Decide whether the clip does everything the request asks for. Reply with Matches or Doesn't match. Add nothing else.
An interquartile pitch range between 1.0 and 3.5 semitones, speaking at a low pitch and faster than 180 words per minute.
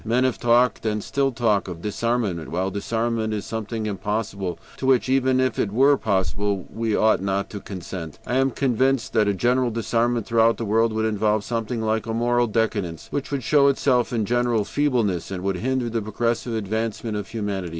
Matches